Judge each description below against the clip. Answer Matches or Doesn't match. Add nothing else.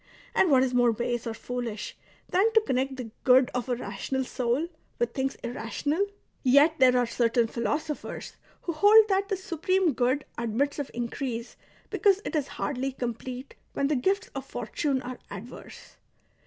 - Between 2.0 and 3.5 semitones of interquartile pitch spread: Doesn't match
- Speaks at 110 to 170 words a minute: Matches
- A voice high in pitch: Matches